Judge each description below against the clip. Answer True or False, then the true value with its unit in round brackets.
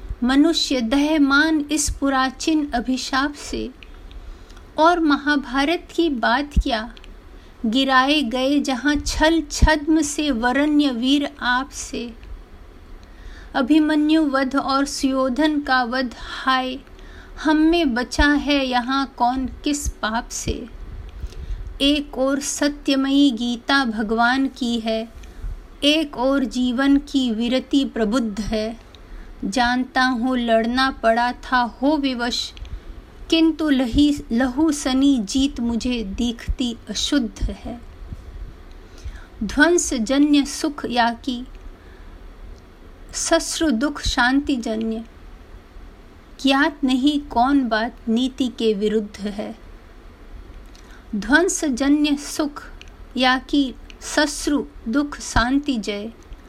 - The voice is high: True (260 Hz)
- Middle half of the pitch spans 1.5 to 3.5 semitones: False (4.3 semitones)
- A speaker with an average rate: False (95 wpm)